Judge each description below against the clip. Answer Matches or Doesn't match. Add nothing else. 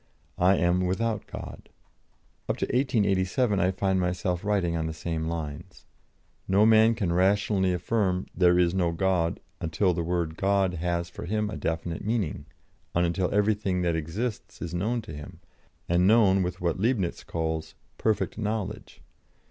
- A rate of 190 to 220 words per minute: Doesn't match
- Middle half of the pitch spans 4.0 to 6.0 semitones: Doesn't match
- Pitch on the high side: Doesn't match